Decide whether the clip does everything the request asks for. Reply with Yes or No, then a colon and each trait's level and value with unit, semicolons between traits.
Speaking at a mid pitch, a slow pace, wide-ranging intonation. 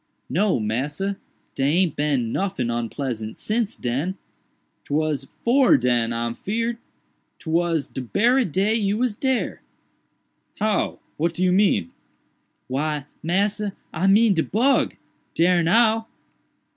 Yes: medium, 175 Hz; slow, 110 wpm; wide, 7.5 semitones